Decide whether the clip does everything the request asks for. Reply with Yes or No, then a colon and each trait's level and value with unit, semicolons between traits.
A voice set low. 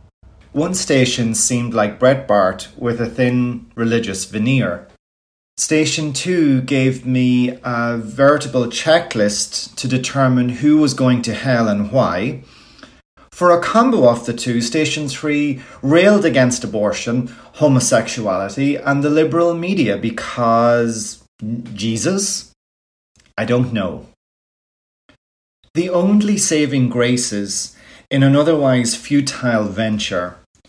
Yes: low, 125 Hz